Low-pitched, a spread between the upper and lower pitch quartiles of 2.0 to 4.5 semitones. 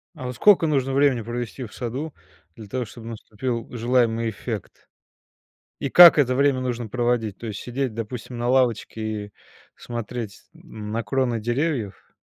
Yes: low, 120 Hz; narrow, 2.5 semitones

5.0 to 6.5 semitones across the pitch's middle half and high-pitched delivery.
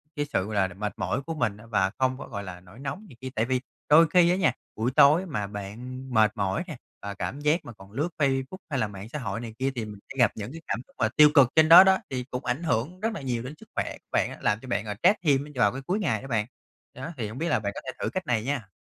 No: wide, 5.6 semitones; low, 130 Hz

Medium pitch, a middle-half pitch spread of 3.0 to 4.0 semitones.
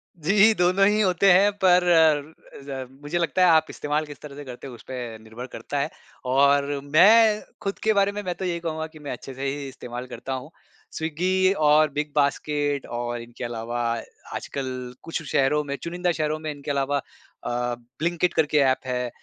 No: medium, 150 Hz; average, 4.8 semitones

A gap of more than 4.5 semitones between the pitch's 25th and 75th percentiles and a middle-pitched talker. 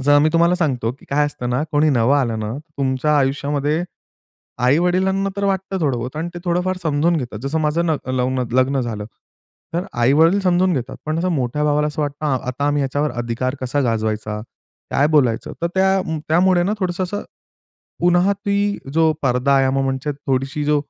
Yes: average, 5.1 semitones; medium, 145 Hz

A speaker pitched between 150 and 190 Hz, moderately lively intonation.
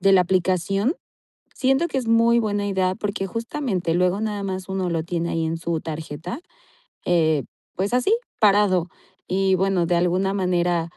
Yes: medium, 185 Hz; average, 3.0 semitones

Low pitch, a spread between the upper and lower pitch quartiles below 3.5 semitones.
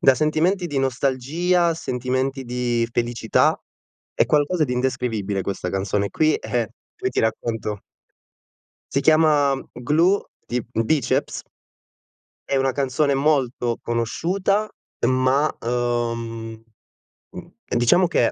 No: low, 130 Hz; average, 4.5 semitones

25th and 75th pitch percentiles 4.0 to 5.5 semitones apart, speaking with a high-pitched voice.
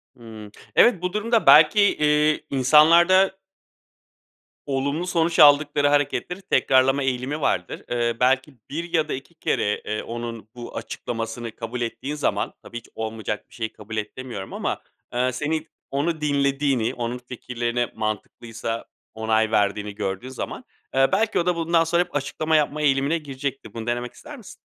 No: average, 4.8 semitones; low, 135 Hz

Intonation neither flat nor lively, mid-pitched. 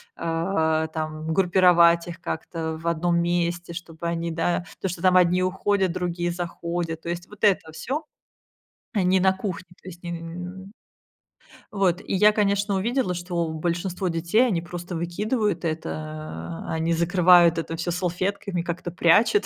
No: narrow, 2.0 semitones; medium, 175 Hz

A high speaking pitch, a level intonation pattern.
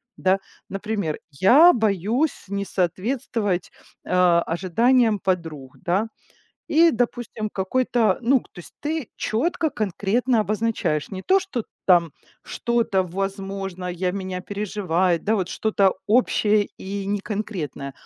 No: high, 200 Hz; average, 3.9 semitones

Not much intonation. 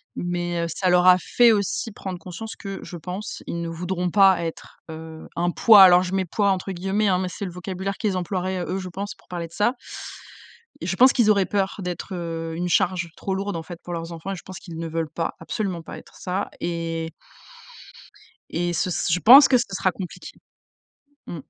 Yes: narrow, 2.3 semitones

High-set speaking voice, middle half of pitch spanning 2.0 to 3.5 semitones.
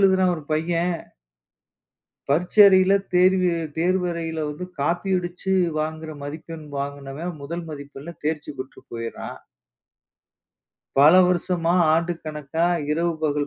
No: medium, 165 Hz; average, 3.0 semitones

